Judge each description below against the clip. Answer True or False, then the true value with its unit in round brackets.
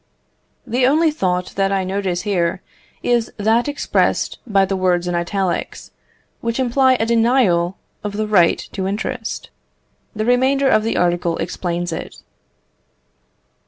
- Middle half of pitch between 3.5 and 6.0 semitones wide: True (4.9 semitones)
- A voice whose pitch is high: True (200 Hz)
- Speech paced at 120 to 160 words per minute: True (135 wpm)